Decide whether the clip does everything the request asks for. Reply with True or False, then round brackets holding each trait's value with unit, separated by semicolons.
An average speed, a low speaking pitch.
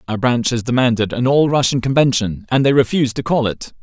False (220 wpm; 125 Hz)